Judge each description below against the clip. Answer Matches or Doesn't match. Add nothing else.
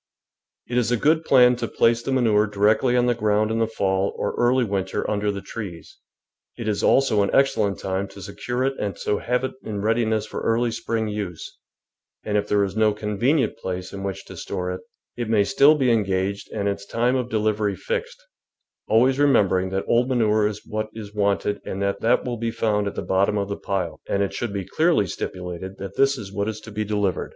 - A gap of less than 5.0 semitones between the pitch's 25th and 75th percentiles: Matches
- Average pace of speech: Doesn't match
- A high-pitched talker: Doesn't match